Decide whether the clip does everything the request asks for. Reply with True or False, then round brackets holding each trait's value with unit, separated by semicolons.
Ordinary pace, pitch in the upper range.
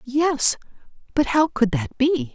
True (155 wpm; 250 Hz)